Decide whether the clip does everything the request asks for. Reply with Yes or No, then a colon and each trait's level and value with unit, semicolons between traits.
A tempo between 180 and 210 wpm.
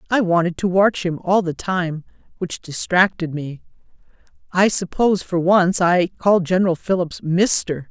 No: average, 150 wpm